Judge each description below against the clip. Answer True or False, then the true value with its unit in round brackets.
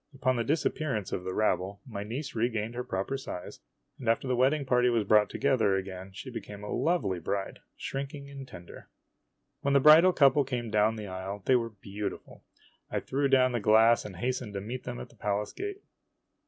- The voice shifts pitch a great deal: False (4.8 semitones)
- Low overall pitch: True (120 Hz)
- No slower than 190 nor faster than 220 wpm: True (200 wpm)